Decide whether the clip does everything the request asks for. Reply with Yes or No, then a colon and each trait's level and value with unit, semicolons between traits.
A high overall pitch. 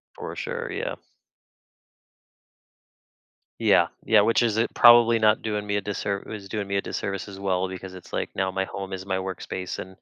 No: low, 100 Hz